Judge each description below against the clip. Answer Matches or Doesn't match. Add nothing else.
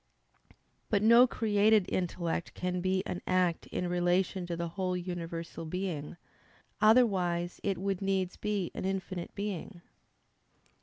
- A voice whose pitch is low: Doesn't match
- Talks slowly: Matches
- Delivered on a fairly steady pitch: Matches